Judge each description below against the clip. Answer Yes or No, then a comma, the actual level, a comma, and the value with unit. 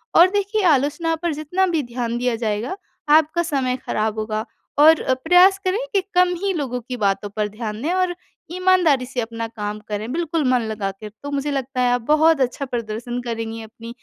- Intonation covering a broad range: Yes, wide, 6.3 semitones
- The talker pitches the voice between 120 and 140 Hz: No, very high, 255 Hz